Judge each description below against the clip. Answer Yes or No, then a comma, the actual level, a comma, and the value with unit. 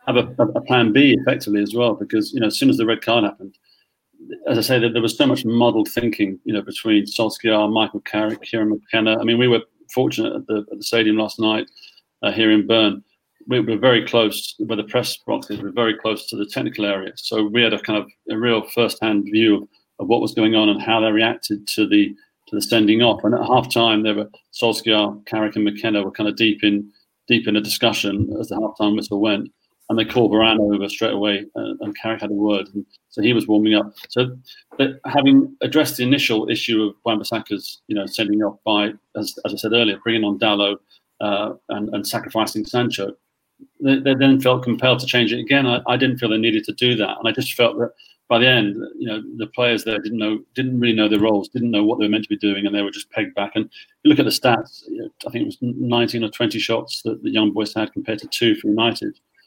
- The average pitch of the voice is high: No, low, 110 Hz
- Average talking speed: No, fast, 240 wpm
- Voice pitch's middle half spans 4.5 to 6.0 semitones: No, average, 2.8 semitones